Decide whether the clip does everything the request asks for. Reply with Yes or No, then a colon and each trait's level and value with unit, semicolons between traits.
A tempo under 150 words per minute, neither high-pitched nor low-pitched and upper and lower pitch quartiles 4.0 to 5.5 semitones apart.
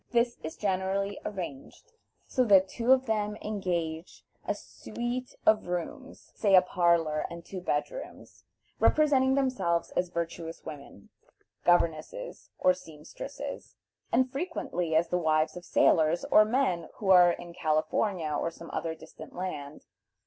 Yes: average, 140 wpm; medium, 180 Hz; average, 4.8 semitones